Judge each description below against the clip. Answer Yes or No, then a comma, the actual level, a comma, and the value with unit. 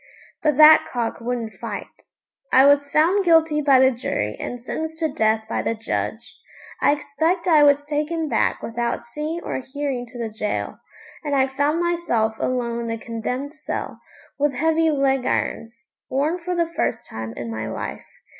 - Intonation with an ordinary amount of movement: Yes, average, 4.9 semitones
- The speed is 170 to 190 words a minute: Yes, average, 175 wpm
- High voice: Yes, very high, 280 Hz